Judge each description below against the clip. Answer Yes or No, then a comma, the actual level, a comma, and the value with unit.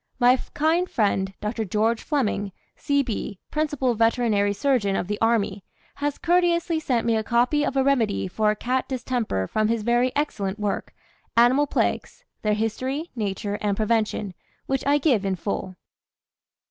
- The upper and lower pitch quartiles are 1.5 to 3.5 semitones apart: No, average, 4.9 semitones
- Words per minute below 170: Yes, average, 150 wpm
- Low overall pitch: No, high, 230 Hz